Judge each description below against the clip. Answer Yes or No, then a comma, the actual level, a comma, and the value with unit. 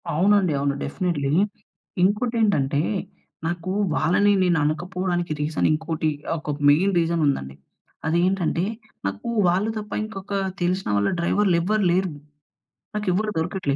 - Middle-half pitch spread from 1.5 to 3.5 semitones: No, average, 3.9 semitones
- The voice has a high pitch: No, medium, 175 Hz